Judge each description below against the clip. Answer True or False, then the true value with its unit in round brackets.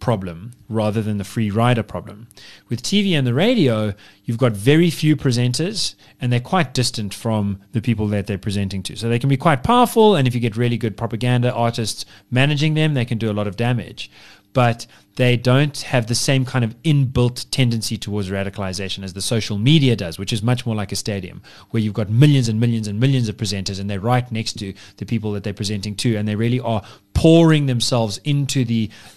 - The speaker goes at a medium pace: False (215 wpm)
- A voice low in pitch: True (115 Hz)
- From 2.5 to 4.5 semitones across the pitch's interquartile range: True (3.5 semitones)